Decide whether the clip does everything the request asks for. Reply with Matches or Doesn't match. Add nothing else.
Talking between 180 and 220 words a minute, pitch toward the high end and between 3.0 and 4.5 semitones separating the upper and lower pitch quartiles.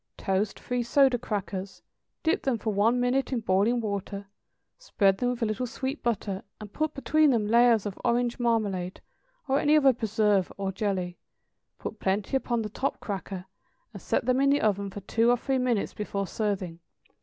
Matches